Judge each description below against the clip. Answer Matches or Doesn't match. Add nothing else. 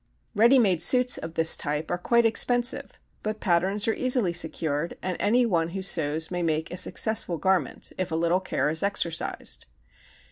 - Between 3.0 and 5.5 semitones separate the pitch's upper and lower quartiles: Matches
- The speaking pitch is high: Doesn't match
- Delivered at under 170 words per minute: Doesn't match